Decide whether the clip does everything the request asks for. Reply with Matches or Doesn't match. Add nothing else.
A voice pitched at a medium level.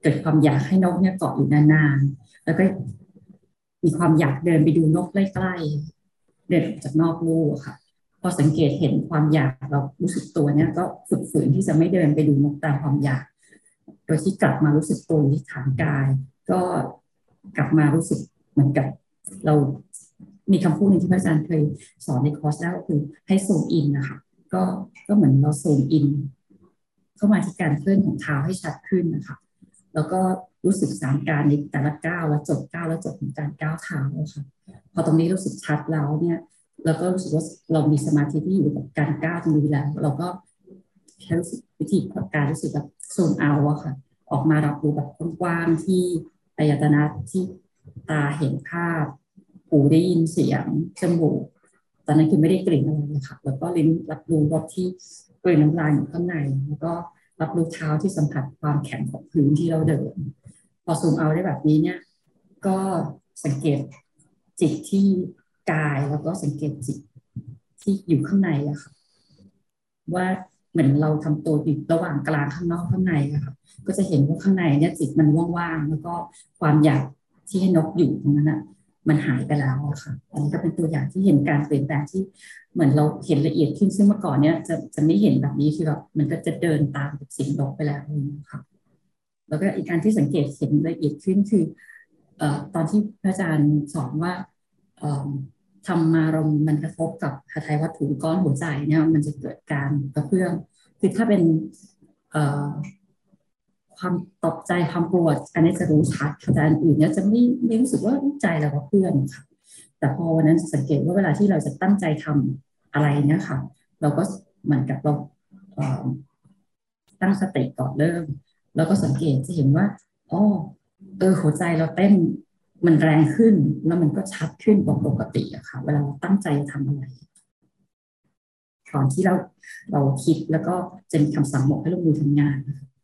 Matches